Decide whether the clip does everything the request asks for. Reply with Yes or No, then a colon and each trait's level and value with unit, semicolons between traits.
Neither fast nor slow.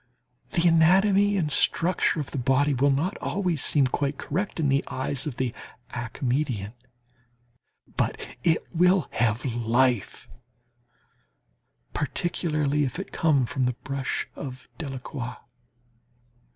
No: slow, 120 wpm